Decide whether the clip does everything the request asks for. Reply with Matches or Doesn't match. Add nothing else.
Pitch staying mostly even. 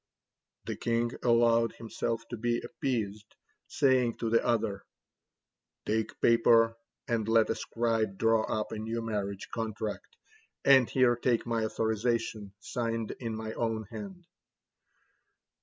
Matches